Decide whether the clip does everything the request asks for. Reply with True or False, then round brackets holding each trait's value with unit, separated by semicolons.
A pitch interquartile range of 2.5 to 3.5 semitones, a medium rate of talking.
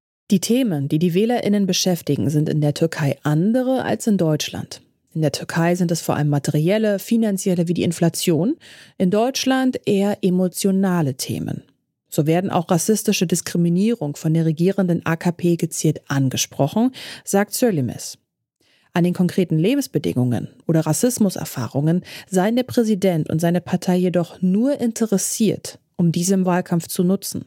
False (4.0 semitones; 140 wpm)